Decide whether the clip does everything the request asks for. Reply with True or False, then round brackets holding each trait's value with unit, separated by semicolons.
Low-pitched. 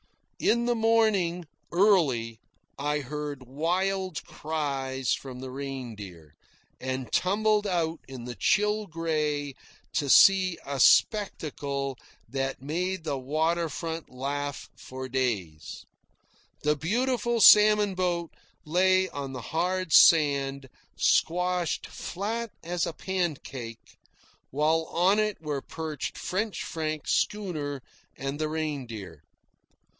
False (155 Hz)